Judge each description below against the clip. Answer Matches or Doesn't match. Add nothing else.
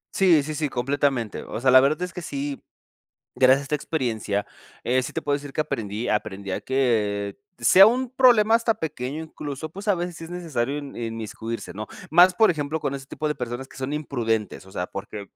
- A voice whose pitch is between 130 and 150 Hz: Matches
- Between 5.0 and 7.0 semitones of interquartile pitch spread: Matches